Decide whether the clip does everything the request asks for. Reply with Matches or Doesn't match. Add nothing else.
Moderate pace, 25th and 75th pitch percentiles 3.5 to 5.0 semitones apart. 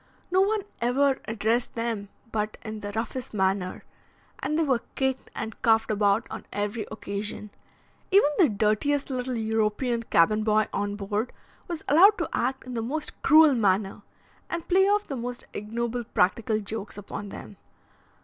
Matches